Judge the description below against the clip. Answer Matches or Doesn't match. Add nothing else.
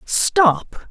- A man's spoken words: Doesn't match